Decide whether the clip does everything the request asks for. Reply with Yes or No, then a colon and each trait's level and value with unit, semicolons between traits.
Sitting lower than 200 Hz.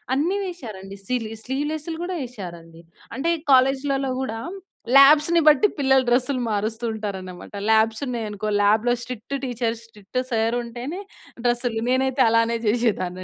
No: high, 240 Hz